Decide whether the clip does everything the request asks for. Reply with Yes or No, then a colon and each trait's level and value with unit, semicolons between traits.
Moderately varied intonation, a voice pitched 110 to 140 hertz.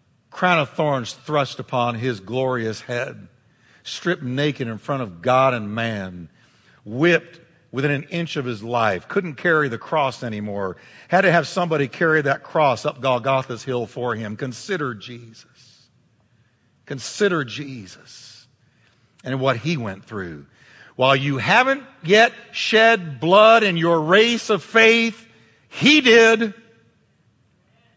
No: wide, 6.1 semitones; low, 135 Hz